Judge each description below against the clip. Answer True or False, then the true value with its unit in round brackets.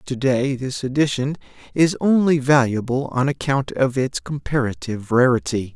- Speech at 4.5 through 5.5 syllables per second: True (4.8 syllables/s)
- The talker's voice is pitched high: False (135 Hz)